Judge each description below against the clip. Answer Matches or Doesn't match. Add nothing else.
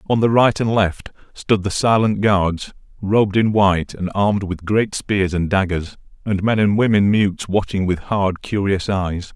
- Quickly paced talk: Doesn't match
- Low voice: Matches